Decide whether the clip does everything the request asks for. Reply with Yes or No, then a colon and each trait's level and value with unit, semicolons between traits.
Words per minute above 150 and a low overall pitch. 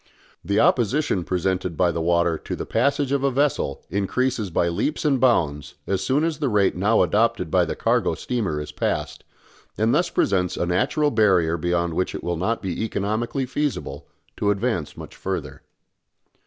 Yes: average, 175 wpm; low, 100 Hz